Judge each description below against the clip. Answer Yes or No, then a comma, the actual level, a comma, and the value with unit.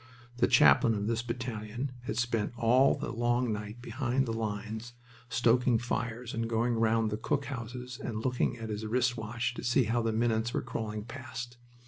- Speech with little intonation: Yes, narrow, 1.7 semitones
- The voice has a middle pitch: No, low, 115 Hz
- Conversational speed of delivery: Yes, average, 180 wpm